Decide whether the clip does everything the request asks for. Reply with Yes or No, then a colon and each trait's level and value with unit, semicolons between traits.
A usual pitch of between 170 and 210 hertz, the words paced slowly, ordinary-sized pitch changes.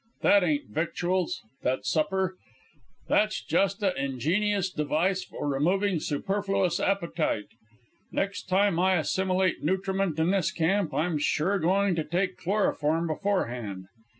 Yes: medium, 185 Hz; slow, 125 wpm; average, 3.9 semitones